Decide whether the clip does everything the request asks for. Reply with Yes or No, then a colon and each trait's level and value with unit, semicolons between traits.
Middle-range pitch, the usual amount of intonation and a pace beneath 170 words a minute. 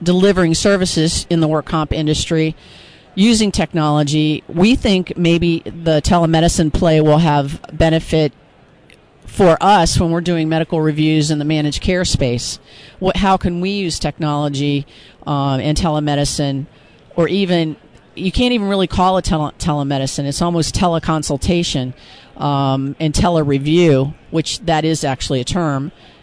Yes: medium, 160 Hz; average, 3.1 semitones; average, 150 wpm